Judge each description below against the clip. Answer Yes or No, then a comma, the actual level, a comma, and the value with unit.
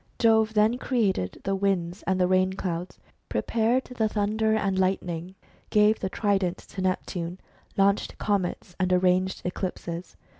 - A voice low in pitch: No, high, 190 Hz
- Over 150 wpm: No, average, 145 wpm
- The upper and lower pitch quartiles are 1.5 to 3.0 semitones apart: Yes, average, 2.7 semitones